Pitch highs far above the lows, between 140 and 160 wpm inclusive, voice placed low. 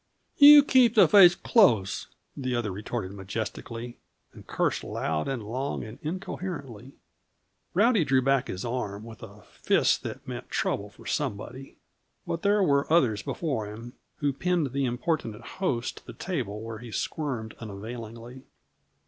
Yes: wide, 6.5 semitones; average, 150 wpm; low, 125 Hz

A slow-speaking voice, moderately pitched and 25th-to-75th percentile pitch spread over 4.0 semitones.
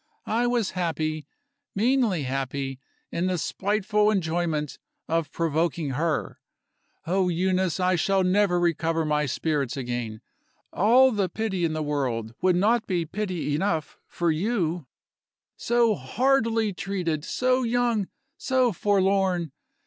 Yes: slow, 125 wpm; medium, 180 Hz; average, 5.0 semitones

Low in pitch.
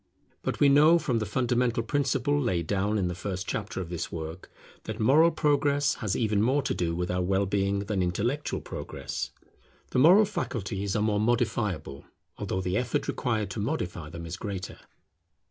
Yes: low, 105 Hz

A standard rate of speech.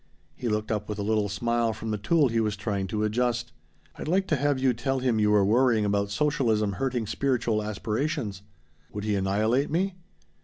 Yes: average, 195 wpm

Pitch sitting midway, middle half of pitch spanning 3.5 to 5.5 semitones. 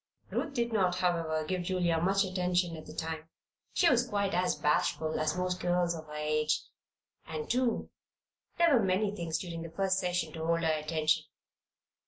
No: medium, 175 Hz; average, 3.0 semitones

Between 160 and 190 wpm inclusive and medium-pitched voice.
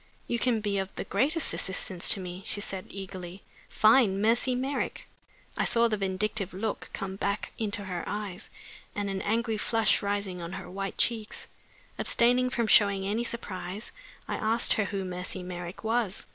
No: average, 170 wpm; high, 205 Hz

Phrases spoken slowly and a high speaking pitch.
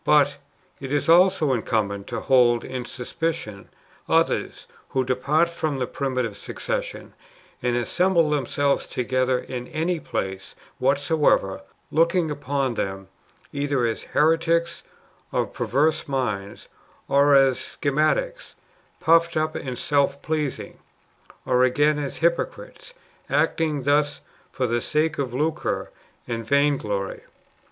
No: slow, 120 wpm; medium, 140 Hz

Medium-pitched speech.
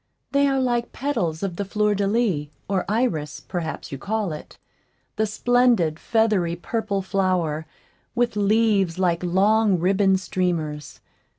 No: high, 195 Hz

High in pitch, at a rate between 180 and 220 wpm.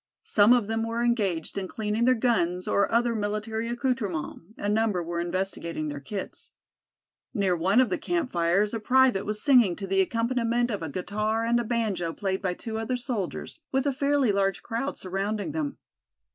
Yes: high, 215 Hz; average, 185 wpm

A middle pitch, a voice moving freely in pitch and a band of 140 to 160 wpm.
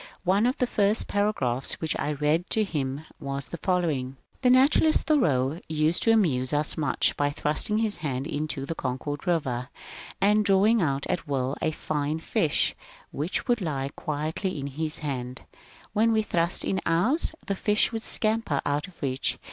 No: medium, 160 Hz; wide, 6.5 semitones; average, 180 wpm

